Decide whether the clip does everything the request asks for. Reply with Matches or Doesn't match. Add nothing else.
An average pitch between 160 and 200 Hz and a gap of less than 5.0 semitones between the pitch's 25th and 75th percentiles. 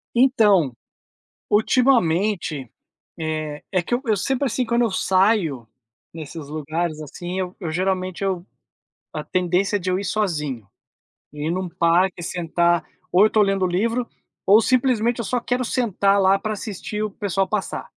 Matches